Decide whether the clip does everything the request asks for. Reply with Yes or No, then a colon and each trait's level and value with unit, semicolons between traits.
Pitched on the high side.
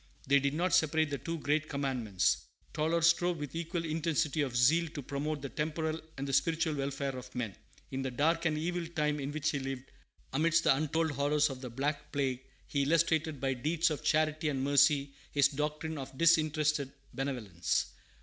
No: medium, 150 Hz